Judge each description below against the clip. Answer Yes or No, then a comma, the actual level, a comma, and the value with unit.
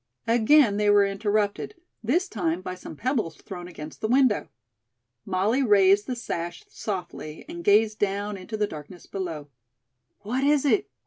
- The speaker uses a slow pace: No, average, 150 wpm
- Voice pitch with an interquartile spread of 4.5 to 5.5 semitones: No, average, 3.8 semitones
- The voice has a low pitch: No, high, 205 Hz